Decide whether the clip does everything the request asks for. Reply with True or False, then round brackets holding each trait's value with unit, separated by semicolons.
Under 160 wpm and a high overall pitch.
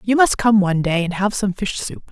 False (285 wpm; 200 Hz)